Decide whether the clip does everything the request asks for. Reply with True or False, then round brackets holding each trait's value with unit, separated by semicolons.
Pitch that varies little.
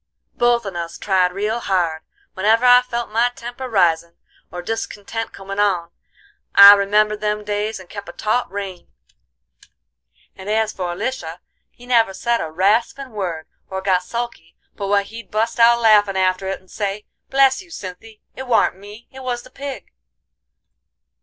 False (3.7 semitones)